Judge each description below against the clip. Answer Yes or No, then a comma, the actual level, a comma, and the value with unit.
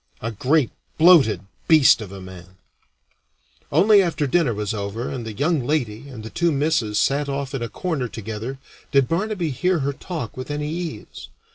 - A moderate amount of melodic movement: No, wide, 6.2 semitones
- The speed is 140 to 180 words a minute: Yes, average, 175 wpm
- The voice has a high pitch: No, low, 135 Hz